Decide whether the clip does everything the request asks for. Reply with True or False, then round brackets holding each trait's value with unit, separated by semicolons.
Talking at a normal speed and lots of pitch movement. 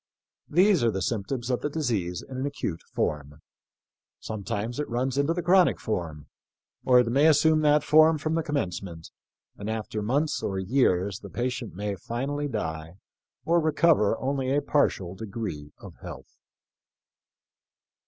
True (150 wpm; 6.9 semitones)